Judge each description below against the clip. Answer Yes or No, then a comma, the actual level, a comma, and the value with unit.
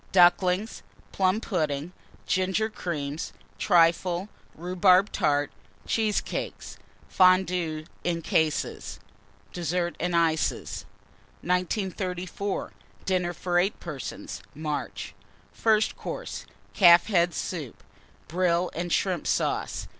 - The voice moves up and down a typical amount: No, narrow, 1.9 semitones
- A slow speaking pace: Yes, slow, 90 wpm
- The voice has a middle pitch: Yes, medium, 180 Hz